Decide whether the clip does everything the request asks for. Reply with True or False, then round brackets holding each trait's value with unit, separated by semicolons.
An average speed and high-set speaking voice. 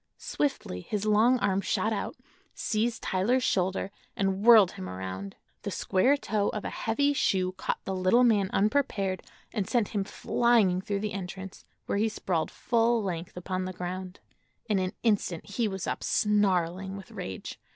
True (165 wpm; 195 Hz)